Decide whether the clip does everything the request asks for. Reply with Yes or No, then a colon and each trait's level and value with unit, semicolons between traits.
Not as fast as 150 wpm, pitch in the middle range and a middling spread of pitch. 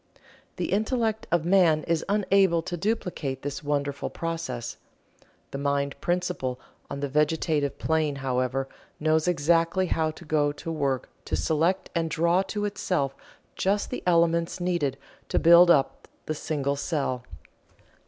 Yes: average, 140 wpm; medium, 160 Hz; average, 3.7 semitones